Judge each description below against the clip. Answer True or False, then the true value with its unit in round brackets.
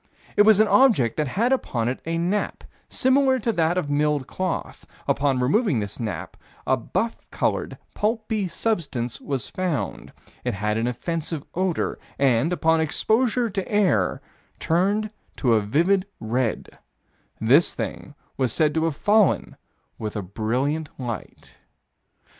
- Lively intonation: True (8.6 semitones)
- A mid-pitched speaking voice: True (160 Hz)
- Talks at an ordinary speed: True (145 wpm)